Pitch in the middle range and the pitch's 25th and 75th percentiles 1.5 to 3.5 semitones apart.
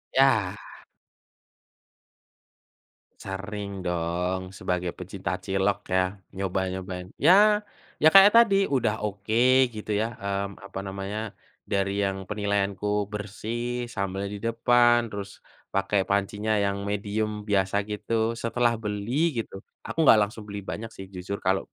No: low, 100 Hz; average, 2.8 semitones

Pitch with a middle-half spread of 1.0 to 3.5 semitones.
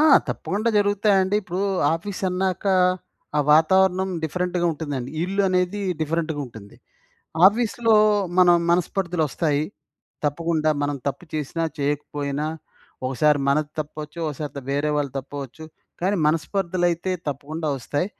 No: average, 4.1 semitones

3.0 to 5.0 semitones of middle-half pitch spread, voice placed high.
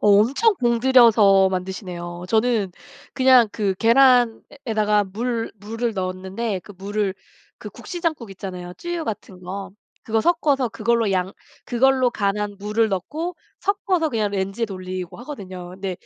Yes: average, 4.3 semitones; high, 215 Hz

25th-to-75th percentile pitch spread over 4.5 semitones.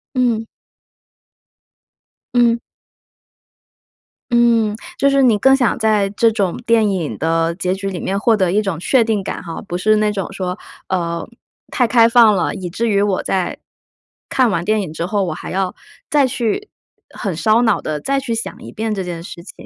No: average, 4.1 semitones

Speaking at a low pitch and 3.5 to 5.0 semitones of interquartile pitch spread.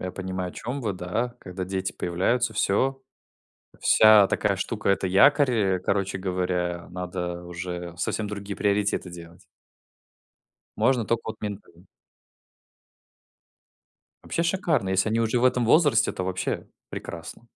Yes: low, 100 Hz; average, 3.9 semitones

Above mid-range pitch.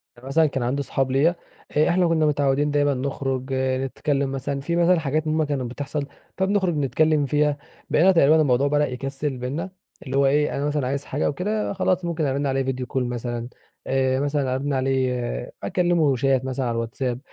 No: medium, 140 Hz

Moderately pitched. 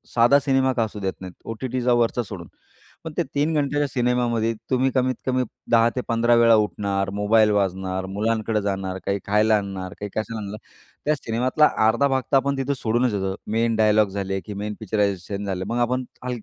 No: low, 115 Hz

